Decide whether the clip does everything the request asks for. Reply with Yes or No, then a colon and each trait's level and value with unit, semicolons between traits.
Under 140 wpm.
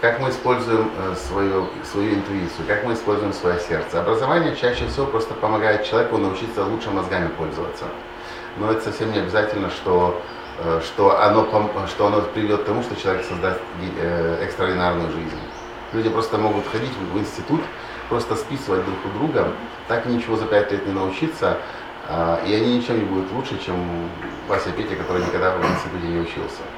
No: fast, 160 wpm